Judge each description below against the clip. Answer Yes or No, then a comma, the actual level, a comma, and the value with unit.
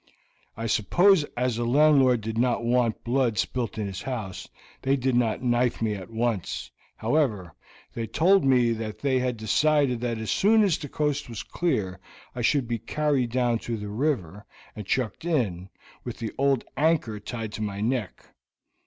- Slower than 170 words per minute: No, average, 175 wpm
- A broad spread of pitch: No, average, 3.8 semitones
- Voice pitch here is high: No, low, 120 Hz